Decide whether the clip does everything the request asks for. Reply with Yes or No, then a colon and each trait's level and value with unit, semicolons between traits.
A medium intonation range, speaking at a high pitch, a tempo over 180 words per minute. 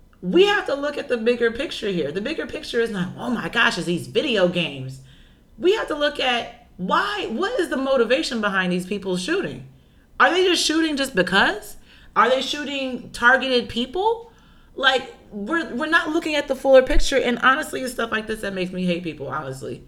No: wide, 7.6 semitones; high, 245 Hz; average, 200 wpm